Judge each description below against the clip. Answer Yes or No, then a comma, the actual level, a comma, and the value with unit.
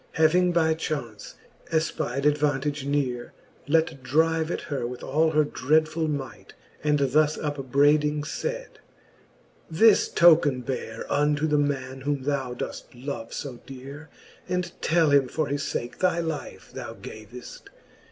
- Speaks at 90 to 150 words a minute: Yes, average, 140 wpm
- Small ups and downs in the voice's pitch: No, average, 3.0 semitones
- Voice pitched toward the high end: No, medium, 145 Hz